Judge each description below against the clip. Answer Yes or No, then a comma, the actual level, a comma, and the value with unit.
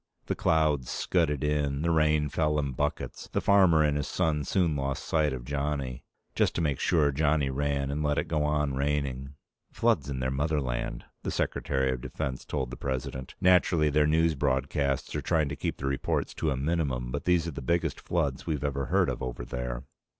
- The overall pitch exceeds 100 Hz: No, very low, 70 Hz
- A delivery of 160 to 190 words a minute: No, average, 200 wpm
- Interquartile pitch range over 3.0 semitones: No, narrow, 2.5 semitones